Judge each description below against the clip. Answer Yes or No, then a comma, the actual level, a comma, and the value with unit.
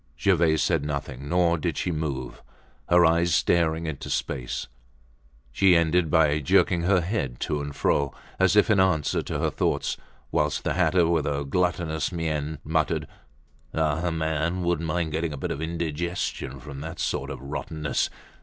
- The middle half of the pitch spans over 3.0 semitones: No, average, 2.7 semitones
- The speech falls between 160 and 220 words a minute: Yes, average, 165 wpm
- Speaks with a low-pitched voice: Yes, very low, 80 Hz